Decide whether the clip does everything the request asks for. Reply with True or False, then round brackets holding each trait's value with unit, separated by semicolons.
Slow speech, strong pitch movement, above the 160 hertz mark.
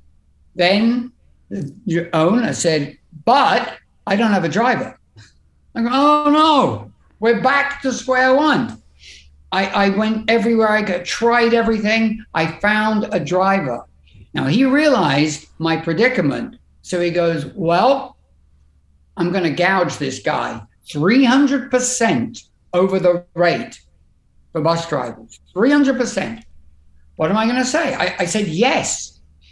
True (130 wpm; 8.2 semitones; 190 Hz)